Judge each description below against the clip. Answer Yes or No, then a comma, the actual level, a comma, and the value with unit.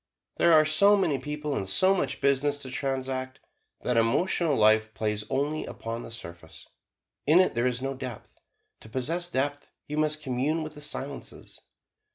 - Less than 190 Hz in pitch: Yes, low, 135 Hz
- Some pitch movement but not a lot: Yes, average, 3.8 semitones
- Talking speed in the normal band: Yes, average, 170 wpm